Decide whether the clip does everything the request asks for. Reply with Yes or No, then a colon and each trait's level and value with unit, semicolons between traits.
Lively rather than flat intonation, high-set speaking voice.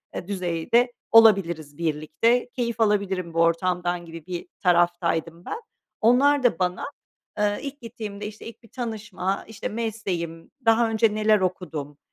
No: average, 4.8 semitones; high, 195 Hz